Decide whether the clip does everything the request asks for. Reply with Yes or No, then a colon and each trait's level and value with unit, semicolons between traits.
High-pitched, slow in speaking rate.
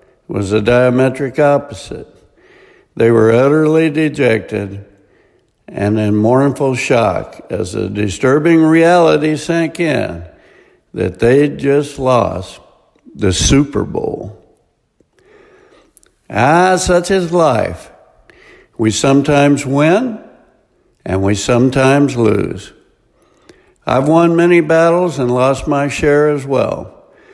No: low, 135 Hz; slow, 100 wpm